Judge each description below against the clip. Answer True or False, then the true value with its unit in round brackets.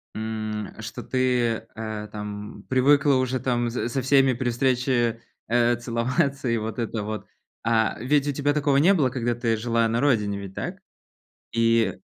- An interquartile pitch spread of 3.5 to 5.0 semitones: False (2.7 semitones)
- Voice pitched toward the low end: True (120 Hz)